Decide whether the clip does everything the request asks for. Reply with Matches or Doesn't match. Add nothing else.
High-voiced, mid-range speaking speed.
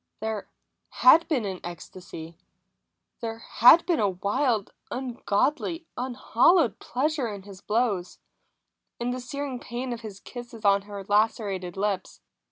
Doesn't match